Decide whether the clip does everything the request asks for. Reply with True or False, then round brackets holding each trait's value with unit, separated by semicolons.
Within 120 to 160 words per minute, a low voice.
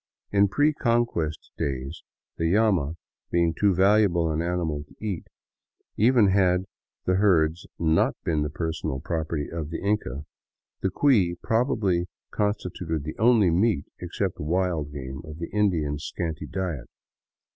True (145 wpm; 85 Hz)